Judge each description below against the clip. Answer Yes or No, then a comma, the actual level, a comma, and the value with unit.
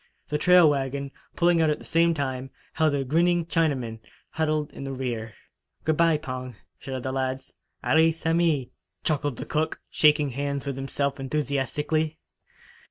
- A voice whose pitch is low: No, medium, 145 Hz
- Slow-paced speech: No, average, 155 wpm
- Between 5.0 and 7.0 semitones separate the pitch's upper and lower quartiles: No, average, 3.0 semitones